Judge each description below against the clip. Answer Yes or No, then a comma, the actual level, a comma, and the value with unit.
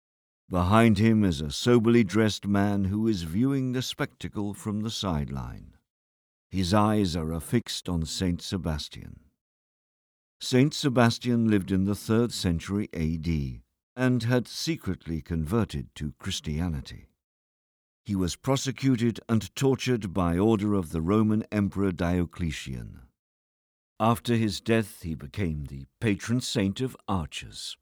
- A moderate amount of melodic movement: No, wide, 5.8 semitones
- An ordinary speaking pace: No, slow, 125 wpm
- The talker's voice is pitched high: No, low, 100 Hz